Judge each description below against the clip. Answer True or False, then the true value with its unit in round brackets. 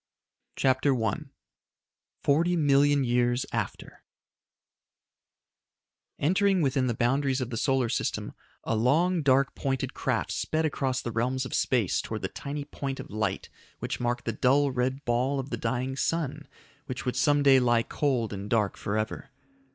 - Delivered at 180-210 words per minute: False (150 wpm)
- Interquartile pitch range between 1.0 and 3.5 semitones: True (2.8 semitones)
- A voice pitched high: False (130 Hz)